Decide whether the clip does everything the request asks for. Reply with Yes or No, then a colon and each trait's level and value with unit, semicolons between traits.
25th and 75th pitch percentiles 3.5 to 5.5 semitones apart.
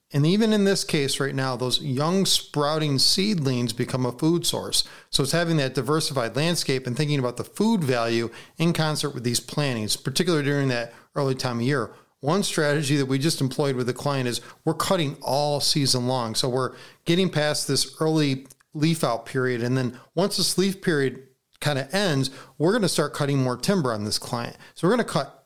Yes: average, 3.8 semitones